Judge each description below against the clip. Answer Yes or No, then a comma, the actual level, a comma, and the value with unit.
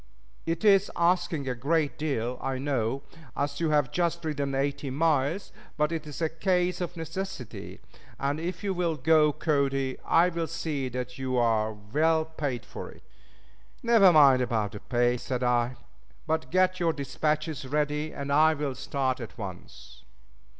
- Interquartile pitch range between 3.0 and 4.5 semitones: Yes, average, 4.1 semitones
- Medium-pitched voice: Yes, medium, 145 Hz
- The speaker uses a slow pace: No, average, 155 wpm